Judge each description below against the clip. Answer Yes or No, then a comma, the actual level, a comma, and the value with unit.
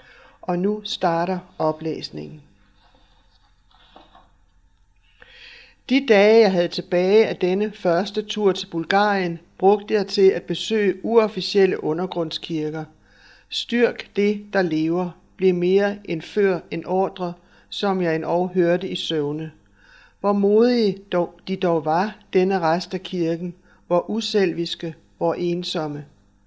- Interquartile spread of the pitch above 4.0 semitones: No, average, 3.6 semitones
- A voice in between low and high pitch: Yes, medium, 180 Hz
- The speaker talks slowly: Yes, slow, 120 wpm